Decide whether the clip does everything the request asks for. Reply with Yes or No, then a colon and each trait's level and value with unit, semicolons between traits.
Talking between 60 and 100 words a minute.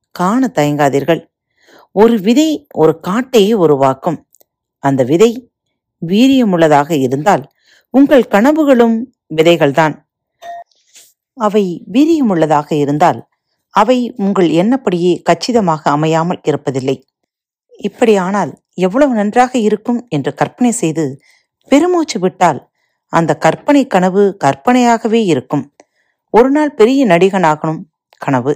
Yes: average, 85 wpm